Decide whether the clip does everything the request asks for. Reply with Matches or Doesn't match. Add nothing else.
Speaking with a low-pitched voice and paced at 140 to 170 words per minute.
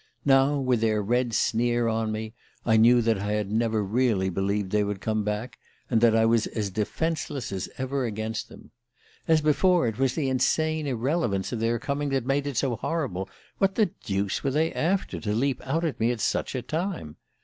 Doesn't match